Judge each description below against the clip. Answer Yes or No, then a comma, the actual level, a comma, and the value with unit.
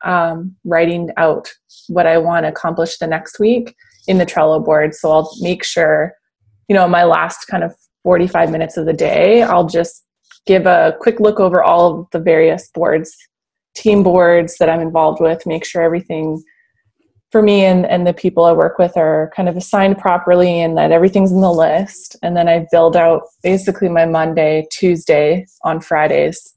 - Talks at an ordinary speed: Yes, average, 185 wpm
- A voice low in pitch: No, medium, 170 Hz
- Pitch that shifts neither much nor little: No, narrow, 2.1 semitones